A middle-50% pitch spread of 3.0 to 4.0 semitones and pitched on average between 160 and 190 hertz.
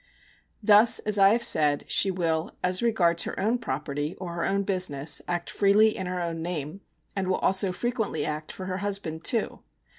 Yes: average, 3.7 semitones; medium, 185 Hz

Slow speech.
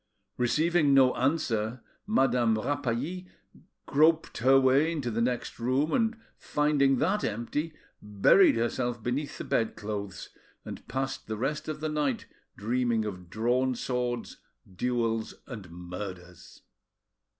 Yes: slow, 120 wpm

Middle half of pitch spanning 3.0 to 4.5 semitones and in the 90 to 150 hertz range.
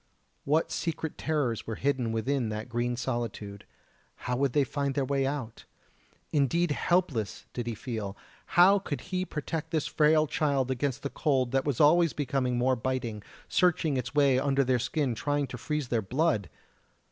Yes: average, 3.8 semitones; low, 135 Hz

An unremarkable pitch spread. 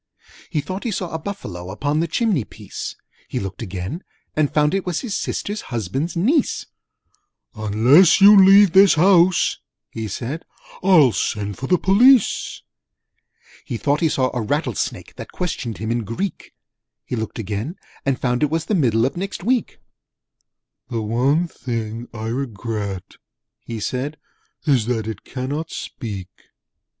No: wide, 8.0 semitones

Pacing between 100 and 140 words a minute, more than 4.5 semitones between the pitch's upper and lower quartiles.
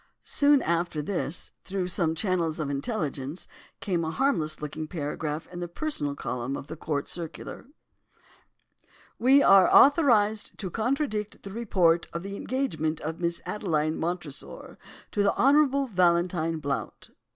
Yes: slow, 135 wpm; wide, 5.4 semitones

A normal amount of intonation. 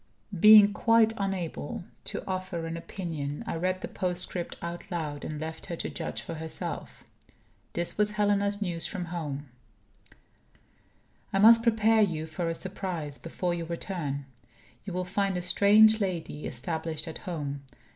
Yes: average, 3.8 semitones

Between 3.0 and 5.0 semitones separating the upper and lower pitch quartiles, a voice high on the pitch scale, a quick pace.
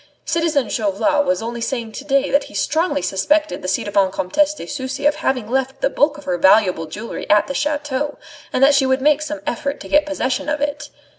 Yes: average, 4.6 semitones; very high, 275 Hz; fast, 220 wpm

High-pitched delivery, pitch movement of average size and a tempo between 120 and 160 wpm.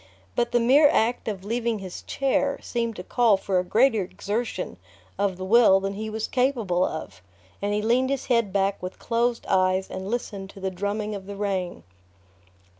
No: high, 210 Hz; average, 3.7 semitones; average, 190 wpm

